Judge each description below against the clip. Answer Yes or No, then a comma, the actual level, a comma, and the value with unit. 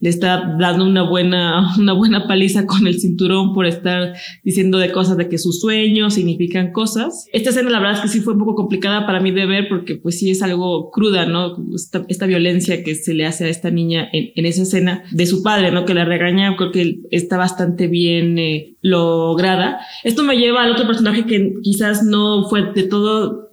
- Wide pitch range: No, average, 2.8 semitones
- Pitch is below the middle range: No, medium, 185 Hz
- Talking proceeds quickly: Yes, fast, 210 wpm